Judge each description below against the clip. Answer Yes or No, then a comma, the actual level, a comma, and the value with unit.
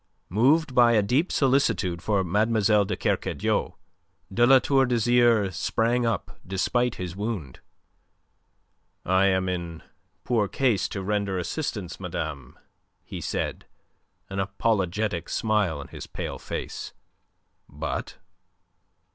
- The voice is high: No, low, 105 Hz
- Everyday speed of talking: No, slow, 115 wpm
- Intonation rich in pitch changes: No, average, 4.5 semitones